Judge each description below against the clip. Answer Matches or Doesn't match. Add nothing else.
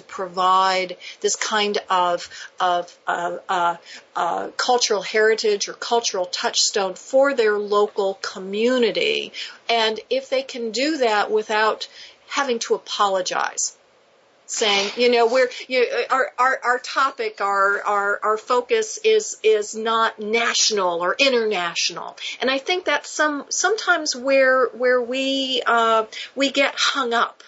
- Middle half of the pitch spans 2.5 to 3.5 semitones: Doesn't match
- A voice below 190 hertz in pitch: Doesn't match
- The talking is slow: Matches